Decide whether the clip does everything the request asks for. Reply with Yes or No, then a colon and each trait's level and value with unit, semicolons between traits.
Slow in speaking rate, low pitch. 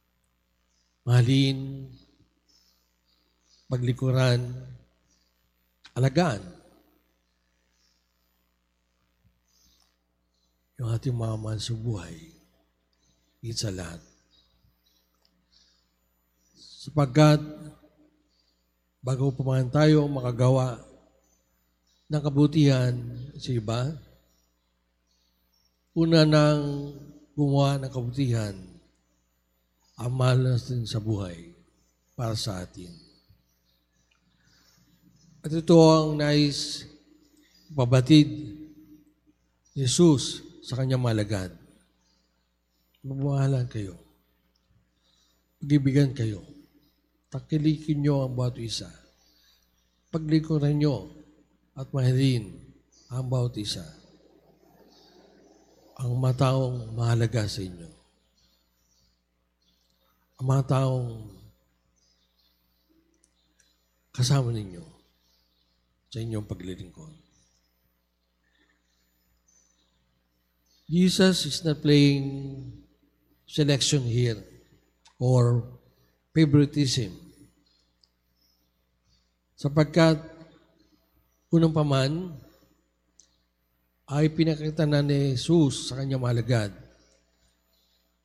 Yes: slow, 65 wpm; low, 100 Hz